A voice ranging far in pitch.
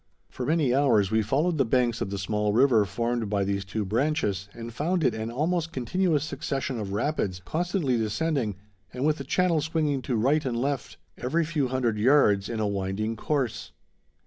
Yes: wide, 5.8 semitones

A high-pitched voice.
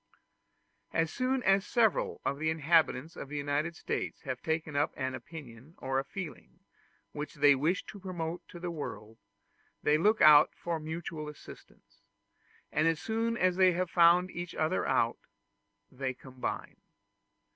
No: medium, 160 Hz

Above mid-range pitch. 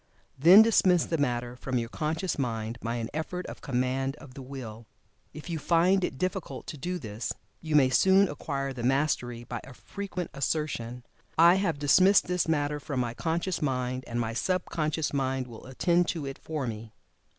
No: medium, 140 Hz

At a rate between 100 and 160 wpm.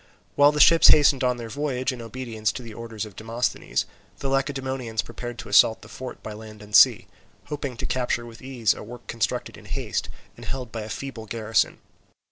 No: average, 200 wpm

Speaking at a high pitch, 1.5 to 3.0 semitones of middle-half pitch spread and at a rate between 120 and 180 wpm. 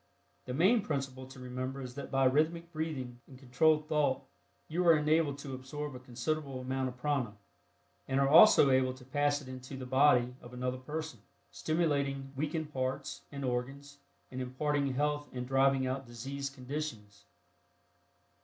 No: low, 135 Hz; narrow, 2.5 semitones; average, 160 wpm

